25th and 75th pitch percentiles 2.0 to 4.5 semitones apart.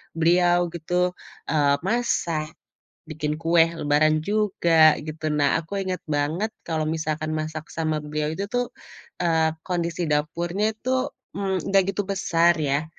Yes: average, 2.7 semitones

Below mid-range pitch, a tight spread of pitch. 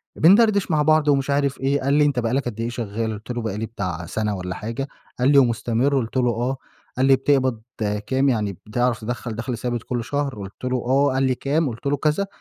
No: low, 125 Hz; average, 3.5 semitones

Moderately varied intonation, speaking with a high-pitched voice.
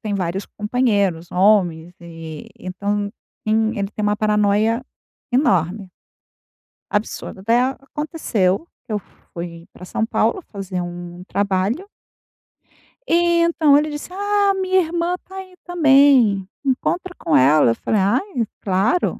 No: wide, 8.0 semitones; high, 210 Hz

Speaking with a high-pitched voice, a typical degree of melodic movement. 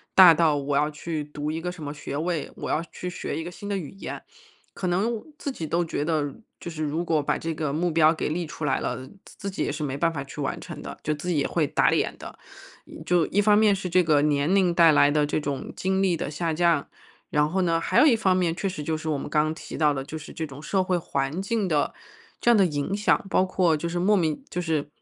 No: medium, 165 Hz; average, 3.3 semitones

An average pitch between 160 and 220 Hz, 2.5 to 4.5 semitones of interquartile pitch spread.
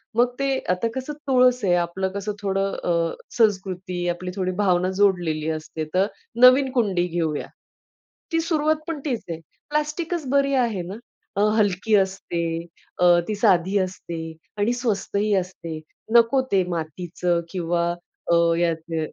No: high, 190 Hz; wide, 5.6 semitones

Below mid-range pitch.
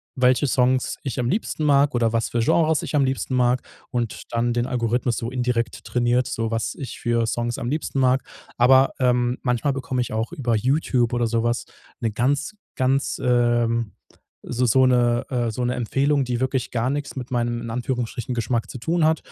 Yes: low, 125 Hz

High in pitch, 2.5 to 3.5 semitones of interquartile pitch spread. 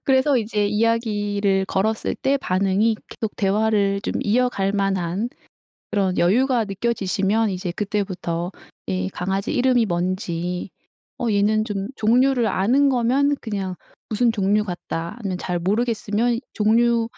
Yes: high, 210 Hz; average, 3.2 semitones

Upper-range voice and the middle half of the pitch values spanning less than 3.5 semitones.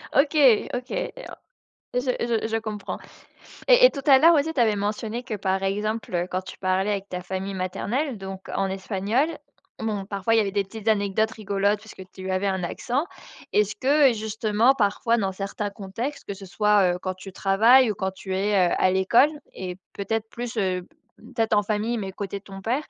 Yes: high, 205 Hz; average, 2.9 semitones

